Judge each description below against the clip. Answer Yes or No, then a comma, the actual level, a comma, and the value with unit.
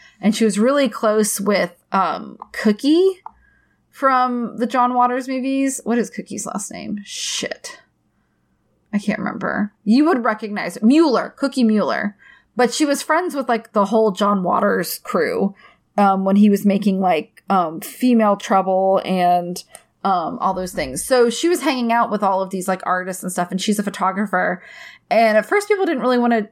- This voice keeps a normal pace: Yes, average, 180 wpm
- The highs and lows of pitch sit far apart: No, average, 4.1 semitones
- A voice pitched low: No, high, 220 Hz